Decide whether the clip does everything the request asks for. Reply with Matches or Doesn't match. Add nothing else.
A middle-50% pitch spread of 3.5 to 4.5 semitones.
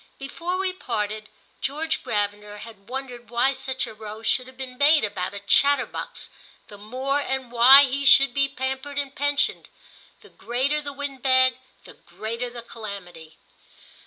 Matches